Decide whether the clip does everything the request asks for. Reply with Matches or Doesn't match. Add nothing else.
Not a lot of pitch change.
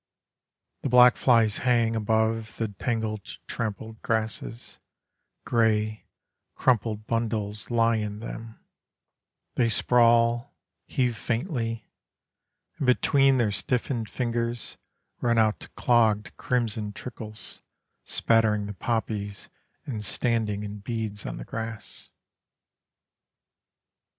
Matches